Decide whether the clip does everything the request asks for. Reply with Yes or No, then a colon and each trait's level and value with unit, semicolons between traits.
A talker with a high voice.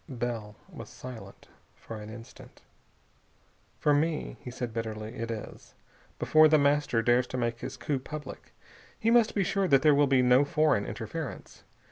No: low, 130 Hz